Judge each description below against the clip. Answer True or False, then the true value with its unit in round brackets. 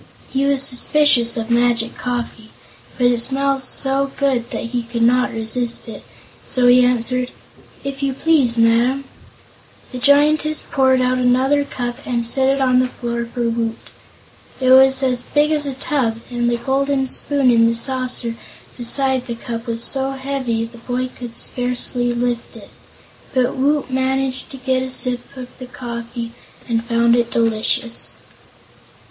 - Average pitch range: False (2.1 semitones)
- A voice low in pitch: False (250 Hz)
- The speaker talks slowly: False (165 wpm)